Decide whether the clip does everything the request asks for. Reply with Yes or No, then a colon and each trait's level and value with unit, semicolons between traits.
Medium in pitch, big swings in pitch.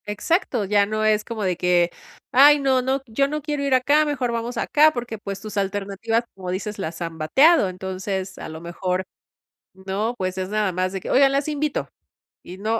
No: high, 210 Hz; wide, 5.9 semitones